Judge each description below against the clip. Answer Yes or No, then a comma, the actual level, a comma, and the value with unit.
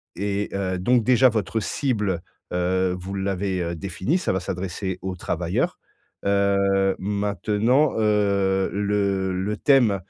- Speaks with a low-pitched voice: Yes, low, 100 Hz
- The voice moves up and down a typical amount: No, narrow, 1.8 semitones